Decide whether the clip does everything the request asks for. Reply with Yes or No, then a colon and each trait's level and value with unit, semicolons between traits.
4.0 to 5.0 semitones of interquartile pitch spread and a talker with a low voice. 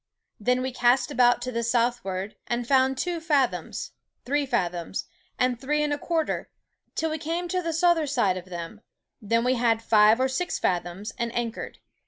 No: average, 4.6 semitones; high, 245 Hz